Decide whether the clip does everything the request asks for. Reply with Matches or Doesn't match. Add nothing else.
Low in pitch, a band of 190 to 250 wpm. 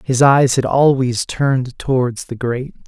Doesn't match